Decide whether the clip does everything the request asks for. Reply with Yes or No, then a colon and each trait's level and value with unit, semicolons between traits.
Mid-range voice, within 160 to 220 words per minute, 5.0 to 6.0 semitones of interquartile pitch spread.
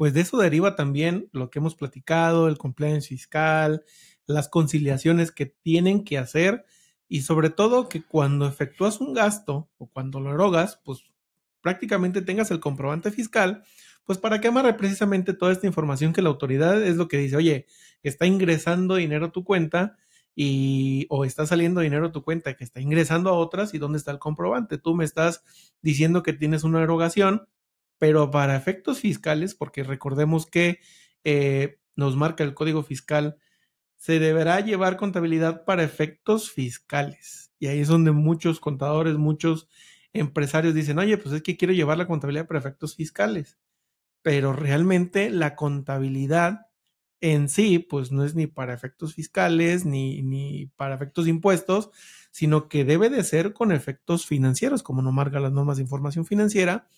No: medium, 160 Hz; average, 165 wpm; average, 3.7 semitones